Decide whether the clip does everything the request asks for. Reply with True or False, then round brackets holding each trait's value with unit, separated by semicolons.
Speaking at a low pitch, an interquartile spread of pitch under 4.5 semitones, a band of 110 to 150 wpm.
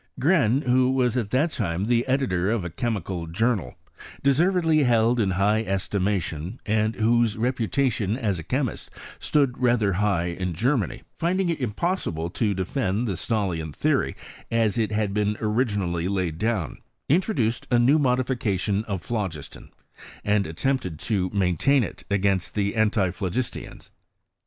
False (110 Hz; 4.8 semitones; 145 wpm)